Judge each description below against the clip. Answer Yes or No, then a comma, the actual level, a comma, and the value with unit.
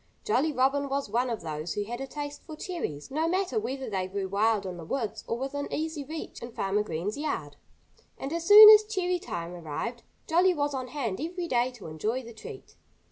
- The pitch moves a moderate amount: No, wide, 7.5 semitones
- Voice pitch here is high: Yes, very high, 260 Hz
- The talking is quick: Yes, fast, 210 wpm